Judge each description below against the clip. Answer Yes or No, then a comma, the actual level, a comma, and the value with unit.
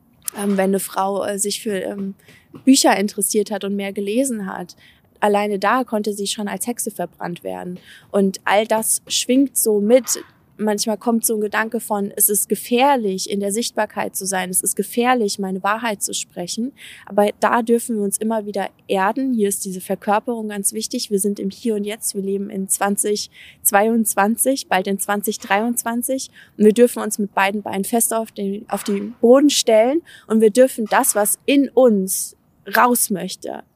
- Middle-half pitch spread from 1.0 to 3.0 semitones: Yes, narrow, 2.5 semitones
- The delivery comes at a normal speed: Yes, average, 180 wpm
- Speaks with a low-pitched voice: No, high, 210 Hz